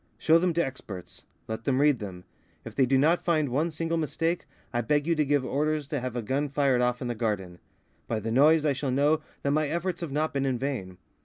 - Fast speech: Yes, fast, 240 wpm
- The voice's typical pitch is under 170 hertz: Yes, medium, 140 Hz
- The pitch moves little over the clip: No, average, 4.0 semitones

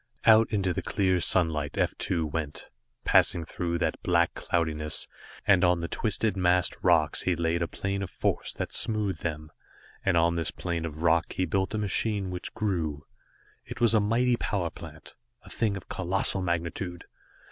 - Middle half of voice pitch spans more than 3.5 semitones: No, average, 3.0 semitones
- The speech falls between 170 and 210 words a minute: Yes, average, 175 wpm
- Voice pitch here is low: Yes, very low, 90 Hz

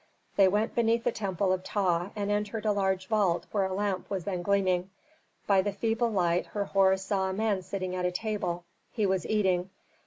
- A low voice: No, high, 195 Hz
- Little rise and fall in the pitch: Yes, narrow, 2.0 semitones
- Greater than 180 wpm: Yes, average, 195 wpm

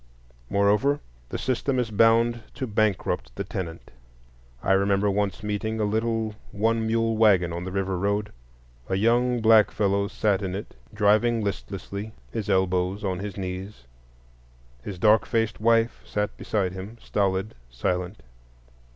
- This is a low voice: Yes, low, 105 Hz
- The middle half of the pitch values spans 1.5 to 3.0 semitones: Yes, narrow, 2.6 semitones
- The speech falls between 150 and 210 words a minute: No, average, 140 wpm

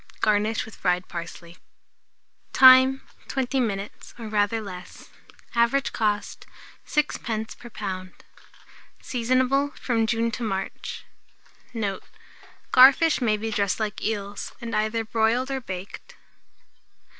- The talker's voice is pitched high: Yes, high, 225 Hz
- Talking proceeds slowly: Yes, slow, 110 wpm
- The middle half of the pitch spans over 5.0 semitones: No, average, 3.6 semitones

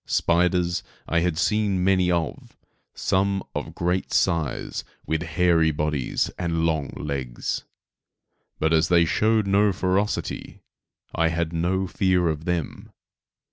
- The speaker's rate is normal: No, slow, 125 wpm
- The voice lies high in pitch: No, very low, 85 Hz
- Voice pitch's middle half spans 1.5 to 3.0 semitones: Yes, narrow, 2.5 semitones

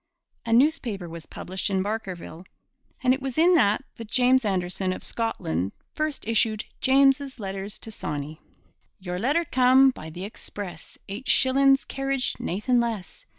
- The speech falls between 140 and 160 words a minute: Yes, average, 150 wpm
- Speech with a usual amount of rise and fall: No, wide, 6.0 semitones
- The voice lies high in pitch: Yes, high, 225 Hz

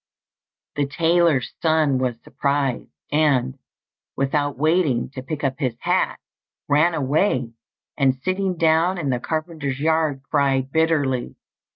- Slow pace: Yes, slow, 125 wpm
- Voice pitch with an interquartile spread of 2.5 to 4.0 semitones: Yes, average, 3.2 semitones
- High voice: No, medium, 145 Hz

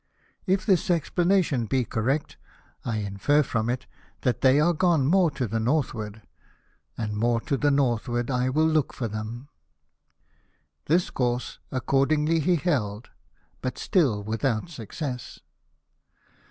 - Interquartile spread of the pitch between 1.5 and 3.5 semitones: No, average, 5.1 semitones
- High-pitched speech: No, low, 130 Hz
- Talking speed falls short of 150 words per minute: Yes, slow, 135 wpm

